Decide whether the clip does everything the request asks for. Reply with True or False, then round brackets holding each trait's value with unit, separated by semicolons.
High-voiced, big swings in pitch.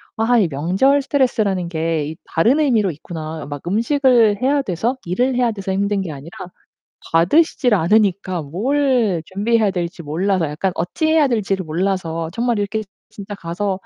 True (195 Hz; 5.8 semitones)